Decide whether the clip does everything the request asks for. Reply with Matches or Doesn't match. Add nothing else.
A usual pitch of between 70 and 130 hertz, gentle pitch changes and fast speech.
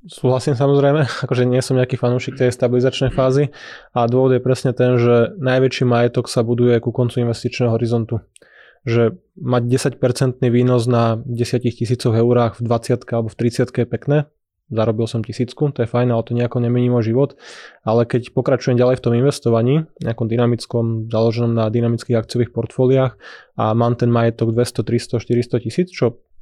Matches